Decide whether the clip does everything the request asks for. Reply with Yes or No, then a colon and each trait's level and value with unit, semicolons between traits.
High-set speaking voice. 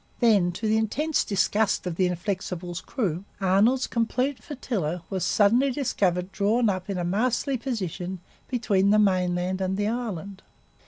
Yes: high, 200 Hz